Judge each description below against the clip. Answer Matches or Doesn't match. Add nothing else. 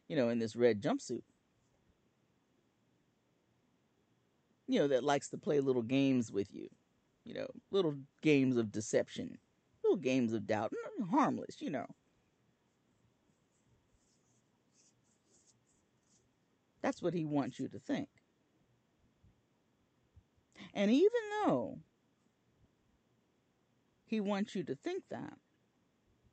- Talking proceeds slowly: Matches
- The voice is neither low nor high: Matches